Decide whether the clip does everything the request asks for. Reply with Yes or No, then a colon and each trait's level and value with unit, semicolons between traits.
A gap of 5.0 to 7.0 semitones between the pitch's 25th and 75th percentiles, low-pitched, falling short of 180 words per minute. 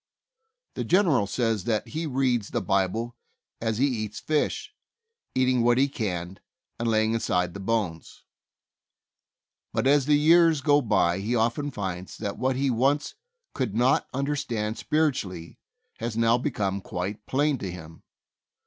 Yes: wide, 5.4 semitones; low, 115 Hz; average, 145 wpm